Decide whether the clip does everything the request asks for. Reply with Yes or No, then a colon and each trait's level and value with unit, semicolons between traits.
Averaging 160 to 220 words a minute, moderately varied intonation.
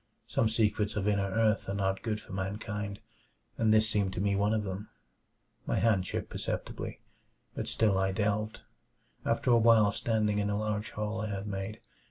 No: average, 185 wpm; narrow, 1.6 semitones